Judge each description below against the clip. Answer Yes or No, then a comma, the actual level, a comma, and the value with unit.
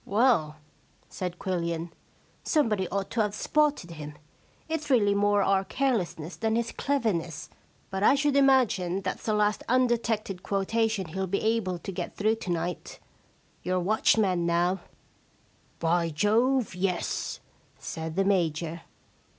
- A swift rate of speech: No, average, 150 wpm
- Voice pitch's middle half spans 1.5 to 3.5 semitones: No, average, 4.6 semitones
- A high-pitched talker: Yes, high, 195 Hz